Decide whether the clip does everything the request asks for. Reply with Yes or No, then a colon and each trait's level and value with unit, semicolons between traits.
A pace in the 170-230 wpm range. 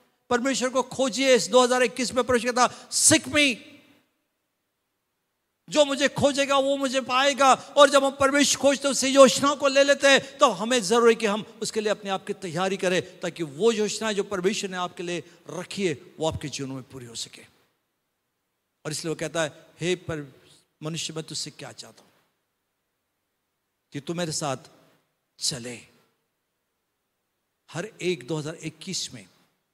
No: average, 155 wpm